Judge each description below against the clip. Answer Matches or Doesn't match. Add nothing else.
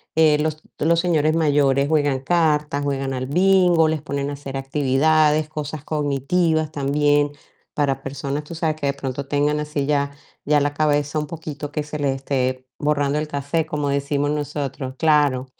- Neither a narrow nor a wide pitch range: Doesn't match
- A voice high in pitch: Doesn't match